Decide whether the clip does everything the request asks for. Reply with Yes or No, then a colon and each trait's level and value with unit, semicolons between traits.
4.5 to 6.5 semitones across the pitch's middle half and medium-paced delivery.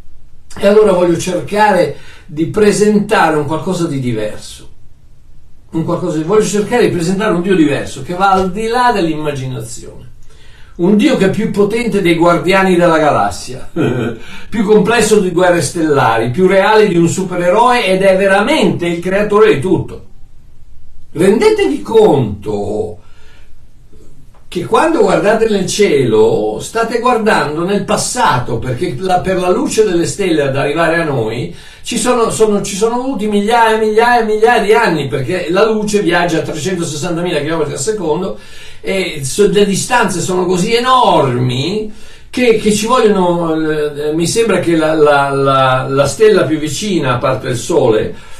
Yes: wide, 5.4 semitones; average, 145 wpm